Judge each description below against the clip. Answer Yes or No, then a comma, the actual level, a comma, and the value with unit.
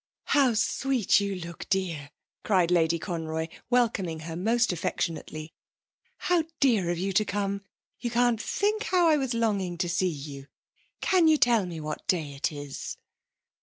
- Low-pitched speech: No, high, 190 Hz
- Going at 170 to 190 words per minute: No, average, 160 wpm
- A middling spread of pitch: No, wide, 6.4 semitones